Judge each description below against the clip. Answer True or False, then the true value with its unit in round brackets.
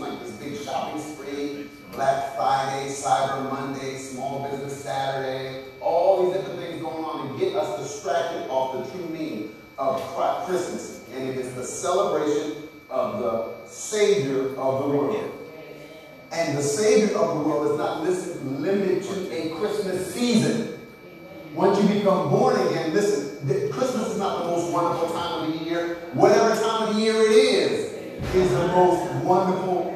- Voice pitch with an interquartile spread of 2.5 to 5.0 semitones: False (5.6 semitones)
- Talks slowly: False (150 wpm)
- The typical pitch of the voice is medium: True (170 Hz)